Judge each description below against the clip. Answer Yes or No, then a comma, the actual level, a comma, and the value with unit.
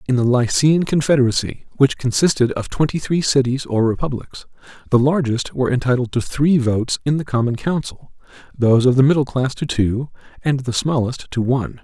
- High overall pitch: No, low, 130 Hz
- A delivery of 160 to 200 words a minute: Yes, average, 175 wpm